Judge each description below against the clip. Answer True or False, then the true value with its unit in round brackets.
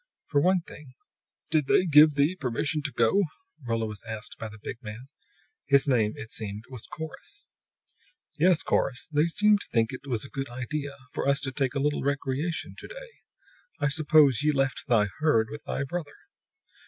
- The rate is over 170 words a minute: True (180 wpm)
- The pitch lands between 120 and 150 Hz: True (140 Hz)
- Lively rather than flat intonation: False (4.2 semitones)